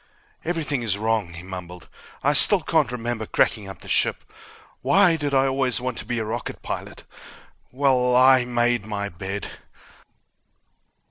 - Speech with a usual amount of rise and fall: Yes, average, 4.6 semitones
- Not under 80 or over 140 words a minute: No, average, 150 wpm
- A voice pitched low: Yes, low, 120 Hz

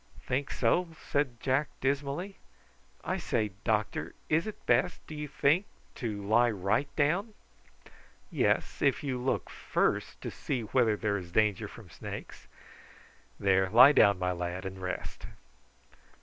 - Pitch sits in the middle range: No, low, 120 Hz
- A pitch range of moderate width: No, wide, 6.1 semitones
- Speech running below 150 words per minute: Yes, average, 140 wpm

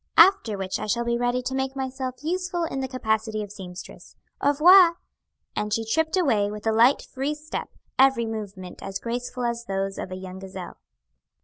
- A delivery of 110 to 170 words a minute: No, average, 190 wpm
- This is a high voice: Yes, high, 235 Hz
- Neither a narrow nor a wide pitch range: Yes, average, 4.7 semitones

